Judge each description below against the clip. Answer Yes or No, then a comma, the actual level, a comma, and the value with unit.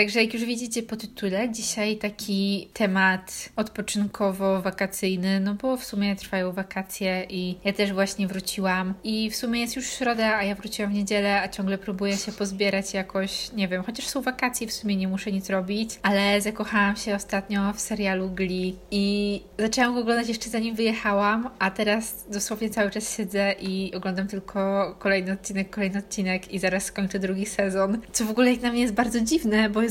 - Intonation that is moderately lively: No, narrow, 2.2 semitones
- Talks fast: Yes, fast, 185 wpm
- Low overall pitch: No, high, 200 Hz